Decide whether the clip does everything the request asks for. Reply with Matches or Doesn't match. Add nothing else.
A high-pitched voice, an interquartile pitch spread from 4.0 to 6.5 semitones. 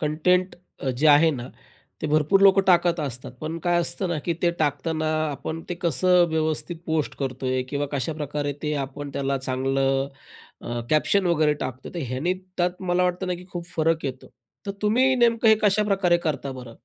Doesn't match